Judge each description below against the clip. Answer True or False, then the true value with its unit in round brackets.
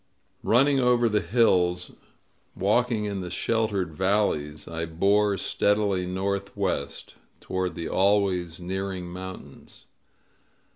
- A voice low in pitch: True (95 Hz)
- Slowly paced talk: True (100 wpm)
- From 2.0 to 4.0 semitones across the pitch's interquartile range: True (2.8 semitones)